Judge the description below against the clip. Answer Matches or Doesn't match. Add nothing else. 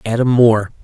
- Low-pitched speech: Matches